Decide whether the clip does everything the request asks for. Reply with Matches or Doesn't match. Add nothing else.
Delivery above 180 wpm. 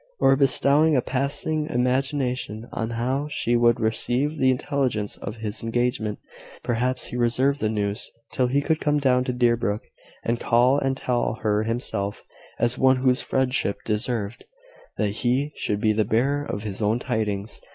Doesn't match